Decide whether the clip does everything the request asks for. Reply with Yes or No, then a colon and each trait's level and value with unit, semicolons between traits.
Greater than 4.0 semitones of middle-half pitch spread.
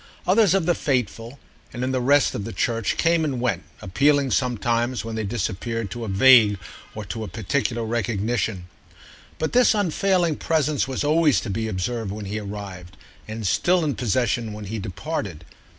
Yes: average, 5.3 semitones